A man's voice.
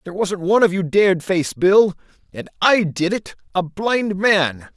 Yes: male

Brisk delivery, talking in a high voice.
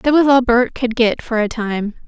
Yes: fast, 260 wpm; high, 235 Hz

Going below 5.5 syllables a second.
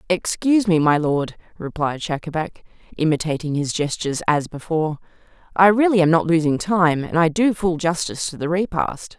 Yes: 5.3 syllables/s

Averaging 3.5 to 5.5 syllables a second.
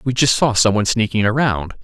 No: 5.8 syllables/s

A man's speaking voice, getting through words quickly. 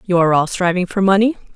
No: female; fast, 230 wpm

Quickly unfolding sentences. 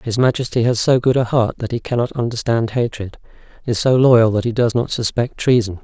Yes: fast, 215 wpm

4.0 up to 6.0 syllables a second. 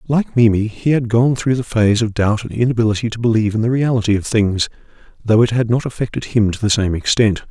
No: 6.2 syllables/s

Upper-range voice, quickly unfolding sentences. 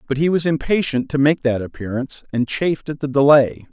No: medium, 140 Hz; fast, 210 wpm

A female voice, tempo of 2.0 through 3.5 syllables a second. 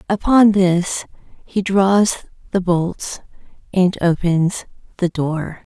Yes: female; 3.0 syllables/s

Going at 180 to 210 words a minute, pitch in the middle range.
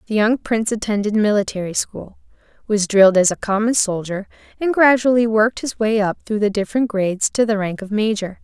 No: average, 190 wpm; high, 210 Hz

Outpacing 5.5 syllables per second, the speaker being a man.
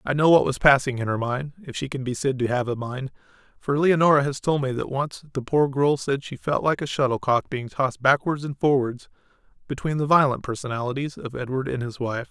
Yes: 5.7 syllables/s; male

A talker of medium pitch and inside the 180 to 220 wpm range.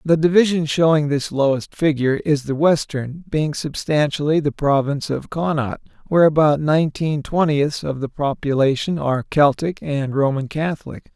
No: medium, 150 Hz; average, 145 wpm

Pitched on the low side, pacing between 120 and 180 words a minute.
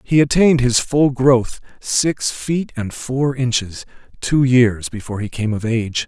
Yes: low, 125 Hz; average, 170 wpm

